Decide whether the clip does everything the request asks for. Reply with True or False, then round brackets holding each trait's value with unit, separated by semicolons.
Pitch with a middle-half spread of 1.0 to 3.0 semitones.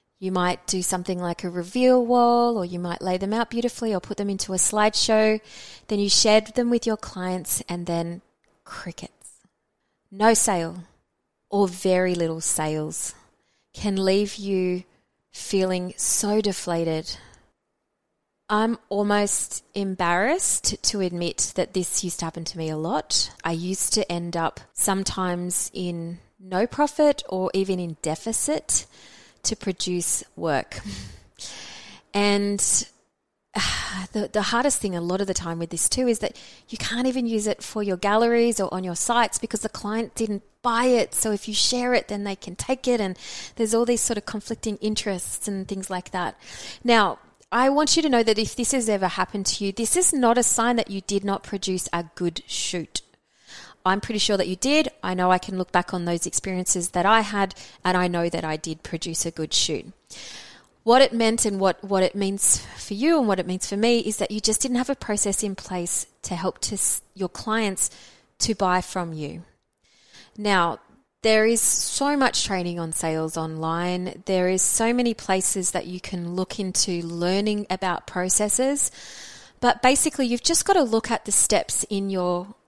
False (3.8 semitones)